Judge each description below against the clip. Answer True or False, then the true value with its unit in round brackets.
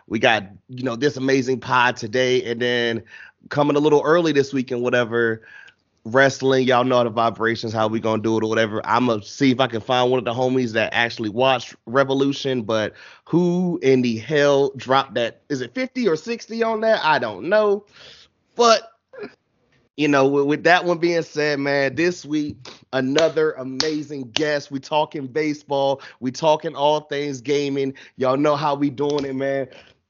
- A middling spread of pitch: True (3.5 semitones)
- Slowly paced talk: False (185 wpm)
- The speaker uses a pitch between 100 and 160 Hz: True (135 Hz)